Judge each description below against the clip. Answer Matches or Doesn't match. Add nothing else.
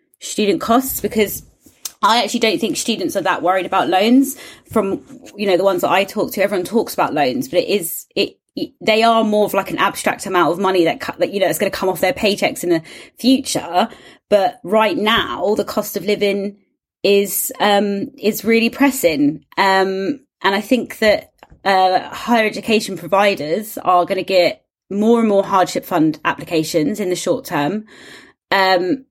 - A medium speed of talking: Matches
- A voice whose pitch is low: Doesn't match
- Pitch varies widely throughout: Doesn't match